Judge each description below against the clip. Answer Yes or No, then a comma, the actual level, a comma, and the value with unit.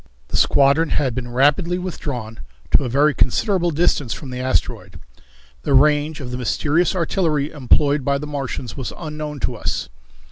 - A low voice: No, medium, 145 Hz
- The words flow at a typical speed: Yes, average, 165 wpm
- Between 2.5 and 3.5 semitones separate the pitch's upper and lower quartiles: Yes, average, 3.1 semitones